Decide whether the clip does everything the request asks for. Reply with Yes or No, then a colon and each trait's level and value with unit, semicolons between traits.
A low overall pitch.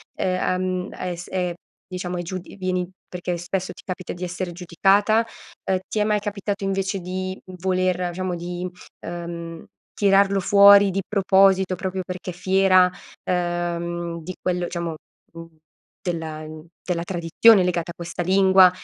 No: medium, 185 Hz